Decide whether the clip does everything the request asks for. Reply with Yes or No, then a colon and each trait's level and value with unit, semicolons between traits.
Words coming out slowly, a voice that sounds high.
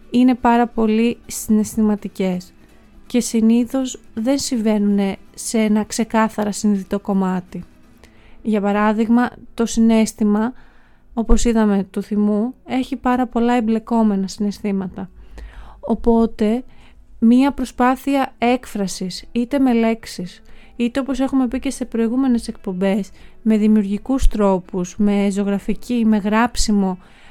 Yes: slow, 105 wpm; high, 225 Hz